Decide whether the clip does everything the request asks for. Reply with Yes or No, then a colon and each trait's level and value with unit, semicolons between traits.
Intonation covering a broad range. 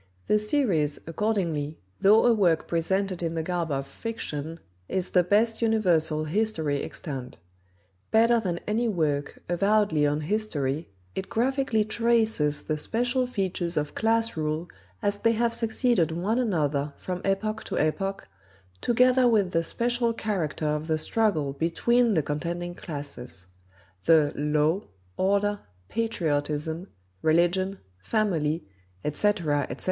Yes: wide, 6.2 semitones